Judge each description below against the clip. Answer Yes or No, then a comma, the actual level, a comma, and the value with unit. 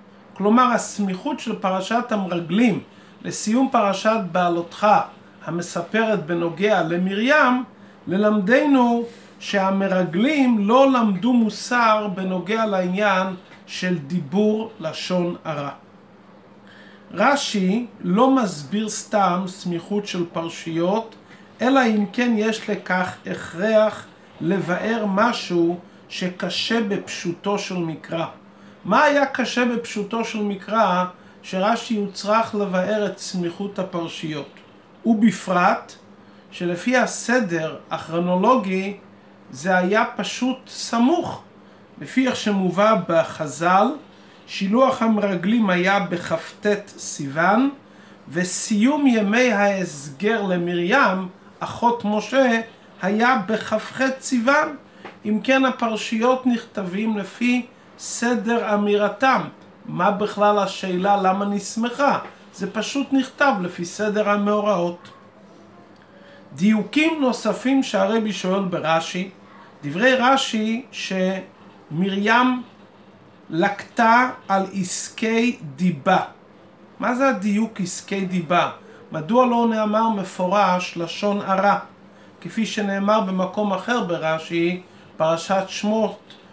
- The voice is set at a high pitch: Yes, high, 205 Hz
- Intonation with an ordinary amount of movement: Yes, average, 3.7 semitones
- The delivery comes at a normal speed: No, slow, 90 wpm